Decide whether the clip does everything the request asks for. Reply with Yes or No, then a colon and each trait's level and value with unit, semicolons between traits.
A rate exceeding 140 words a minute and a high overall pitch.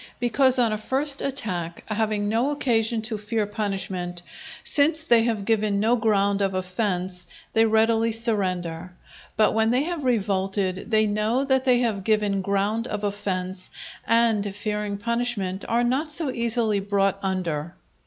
Yes: average, 150 wpm; high, 215 Hz